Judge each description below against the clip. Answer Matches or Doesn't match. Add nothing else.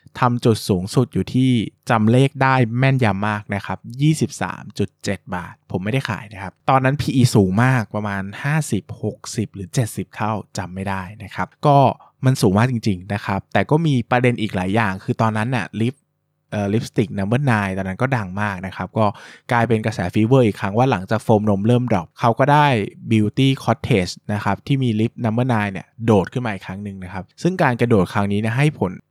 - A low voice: Matches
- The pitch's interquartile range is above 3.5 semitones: Matches